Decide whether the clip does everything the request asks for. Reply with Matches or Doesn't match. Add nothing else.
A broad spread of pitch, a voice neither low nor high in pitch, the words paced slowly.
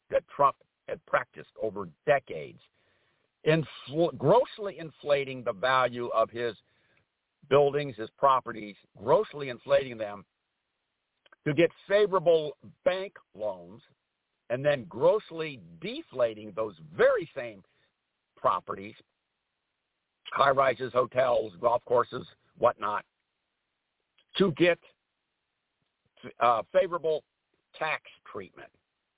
Matches